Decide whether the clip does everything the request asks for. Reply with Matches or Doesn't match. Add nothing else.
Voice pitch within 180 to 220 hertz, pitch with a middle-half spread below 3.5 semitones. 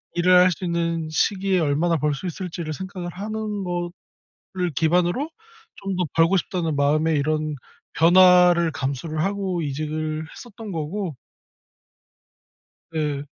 Doesn't match